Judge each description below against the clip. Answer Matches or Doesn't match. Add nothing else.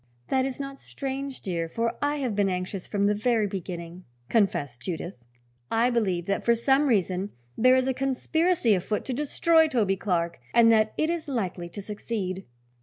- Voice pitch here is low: Doesn't match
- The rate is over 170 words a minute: Matches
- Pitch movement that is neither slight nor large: Doesn't match